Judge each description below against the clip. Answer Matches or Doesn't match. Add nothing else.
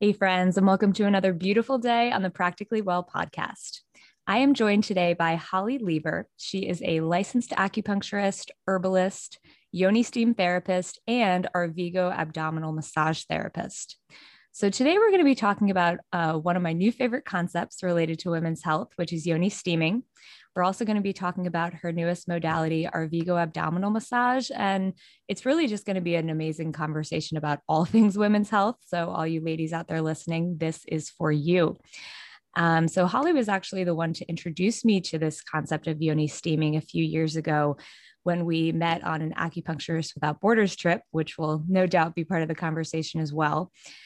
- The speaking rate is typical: Matches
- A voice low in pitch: Doesn't match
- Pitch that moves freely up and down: Doesn't match